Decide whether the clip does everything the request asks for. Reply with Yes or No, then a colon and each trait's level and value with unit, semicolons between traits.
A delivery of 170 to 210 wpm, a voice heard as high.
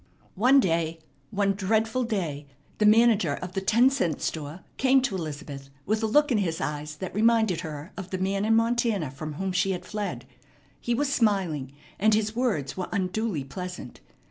Yes: average, 180 wpm; high, 195 Hz